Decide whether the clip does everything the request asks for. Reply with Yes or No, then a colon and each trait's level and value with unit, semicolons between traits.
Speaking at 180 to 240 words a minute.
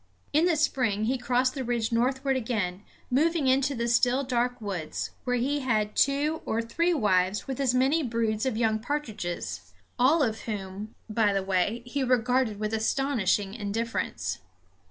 No: average, 160 wpm